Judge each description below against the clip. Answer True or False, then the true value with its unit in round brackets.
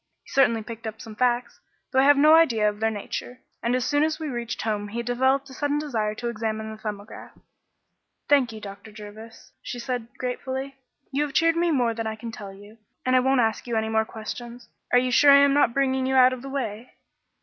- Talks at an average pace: False (230 wpm)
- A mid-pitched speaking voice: False (240 Hz)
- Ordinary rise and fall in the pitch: True (3.5 semitones)